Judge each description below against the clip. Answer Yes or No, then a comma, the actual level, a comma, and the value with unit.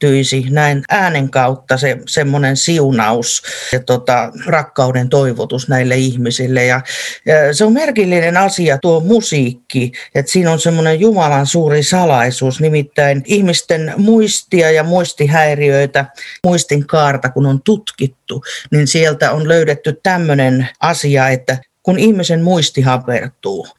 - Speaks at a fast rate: No, average, 120 wpm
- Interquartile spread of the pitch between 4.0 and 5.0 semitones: Yes, average, 4.3 semitones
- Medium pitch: Yes, medium, 145 Hz